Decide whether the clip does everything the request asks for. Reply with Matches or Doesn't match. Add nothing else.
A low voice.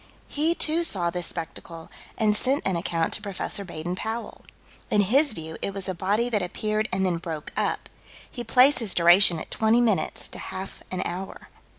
Doesn't match